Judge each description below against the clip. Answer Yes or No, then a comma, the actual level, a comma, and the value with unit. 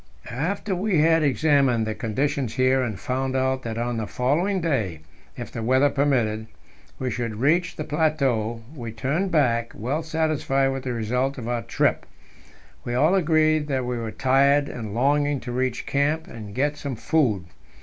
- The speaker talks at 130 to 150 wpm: No, average, 170 wpm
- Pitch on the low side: Yes, low, 130 Hz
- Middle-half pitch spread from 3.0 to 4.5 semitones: Yes, average, 4.2 semitones